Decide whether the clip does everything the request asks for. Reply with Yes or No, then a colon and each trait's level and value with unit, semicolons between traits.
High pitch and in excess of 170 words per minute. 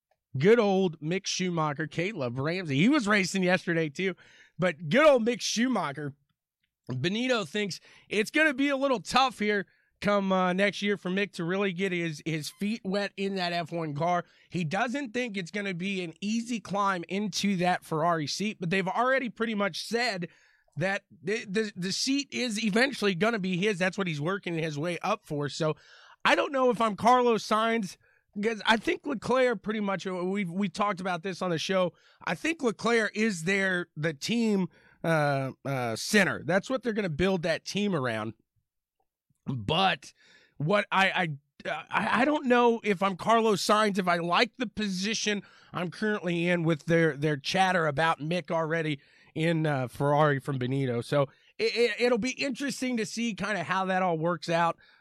Yes: high, 195 Hz; average, 185 wpm